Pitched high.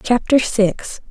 Yes: high, 225 Hz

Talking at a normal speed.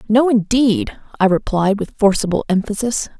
No: slow, 130 wpm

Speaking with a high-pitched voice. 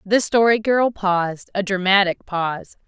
Yes: high, 200 Hz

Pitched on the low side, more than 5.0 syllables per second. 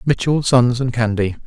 No: low, 125 Hz; 4.7 syllables/s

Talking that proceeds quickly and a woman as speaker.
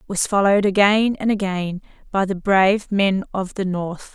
No: average, 190 wpm; female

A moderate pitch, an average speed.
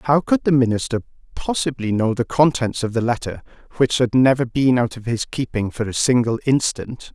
No: low, 125 Hz; average, 195 wpm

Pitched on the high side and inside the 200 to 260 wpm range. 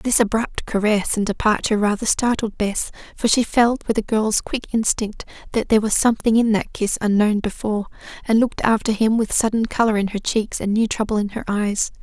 Yes: high, 215 Hz; fast, 205 wpm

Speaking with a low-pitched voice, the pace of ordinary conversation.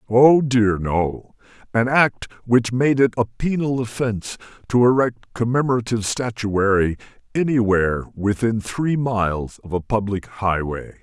No: low, 115 Hz; slow, 125 wpm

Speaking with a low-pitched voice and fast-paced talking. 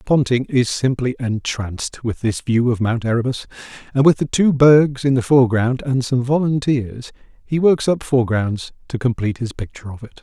No: low, 125 Hz; average, 180 wpm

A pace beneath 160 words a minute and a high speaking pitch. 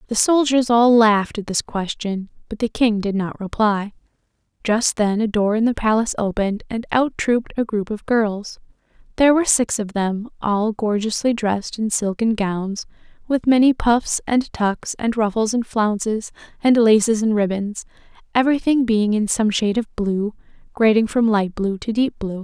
No: average, 175 wpm; high, 220 Hz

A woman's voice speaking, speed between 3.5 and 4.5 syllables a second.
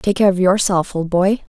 No: female; 4.9 syllables/s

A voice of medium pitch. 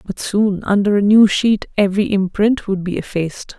No: high, 200 Hz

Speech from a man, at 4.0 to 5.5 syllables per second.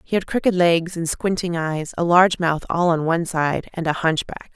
No: female; 5.1 syllables/s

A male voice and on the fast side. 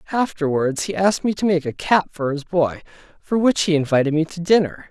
Yes: male; fast, 220 wpm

